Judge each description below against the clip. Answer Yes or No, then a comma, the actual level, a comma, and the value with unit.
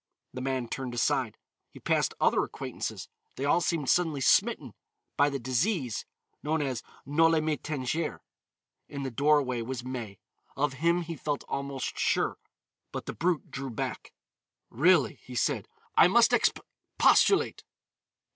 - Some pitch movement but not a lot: Yes, average, 3.5 semitones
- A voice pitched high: No, medium, 140 Hz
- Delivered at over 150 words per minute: No, average, 145 wpm